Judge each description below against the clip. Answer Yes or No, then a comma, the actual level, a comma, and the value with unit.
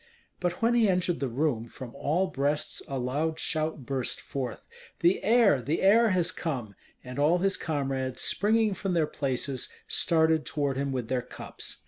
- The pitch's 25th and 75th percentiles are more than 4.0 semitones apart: Yes, average, 5.3 semitones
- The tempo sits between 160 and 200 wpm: Yes, average, 170 wpm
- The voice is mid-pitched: Yes, medium, 150 Hz